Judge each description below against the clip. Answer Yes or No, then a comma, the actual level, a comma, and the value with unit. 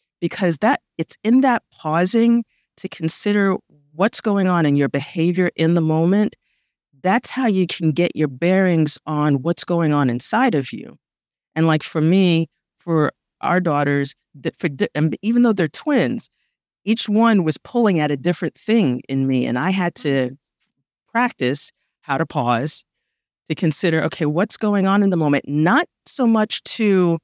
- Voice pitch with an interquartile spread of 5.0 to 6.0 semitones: Yes, wide, 5.4 semitones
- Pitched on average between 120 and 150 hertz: No, medium, 170 Hz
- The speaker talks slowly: No, average, 165 wpm